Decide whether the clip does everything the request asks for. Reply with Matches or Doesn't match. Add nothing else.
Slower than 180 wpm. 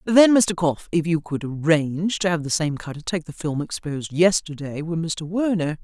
Doesn't match